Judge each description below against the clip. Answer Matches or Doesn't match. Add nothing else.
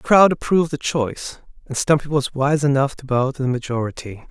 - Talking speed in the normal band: Doesn't match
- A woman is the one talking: Doesn't match